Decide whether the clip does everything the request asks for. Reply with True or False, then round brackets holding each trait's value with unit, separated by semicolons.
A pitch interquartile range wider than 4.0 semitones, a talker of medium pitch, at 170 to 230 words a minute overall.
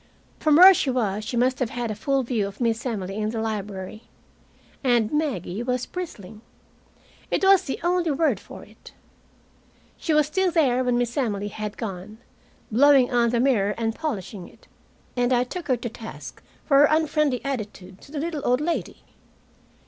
False (5.2 semitones; 245 Hz; 180 wpm)